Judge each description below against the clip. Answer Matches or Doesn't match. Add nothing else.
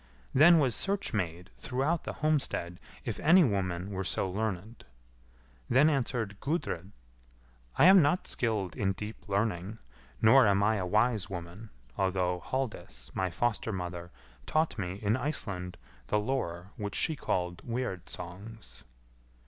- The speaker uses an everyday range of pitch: Doesn't match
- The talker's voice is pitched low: Matches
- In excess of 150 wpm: Doesn't match